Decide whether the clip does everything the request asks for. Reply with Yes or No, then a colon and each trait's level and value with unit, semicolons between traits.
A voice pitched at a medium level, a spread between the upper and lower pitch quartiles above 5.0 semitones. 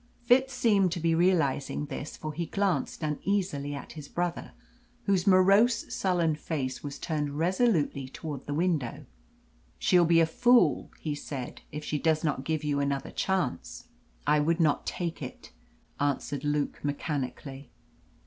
No: medium, 155 Hz; average, 4.1 semitones